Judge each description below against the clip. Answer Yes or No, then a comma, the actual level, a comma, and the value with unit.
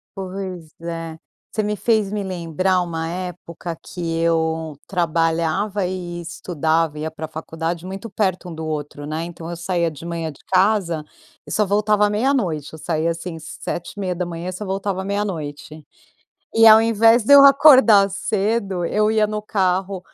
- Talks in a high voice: No, medium, 180 Hz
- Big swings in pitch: No, average, 3.8 semitones